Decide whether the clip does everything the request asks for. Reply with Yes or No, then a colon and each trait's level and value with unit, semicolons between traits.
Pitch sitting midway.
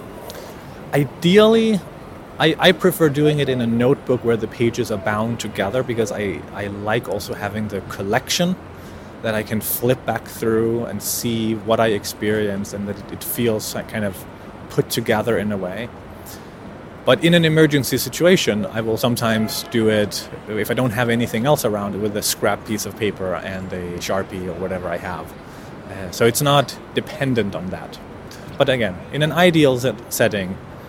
No: low, 110 Hz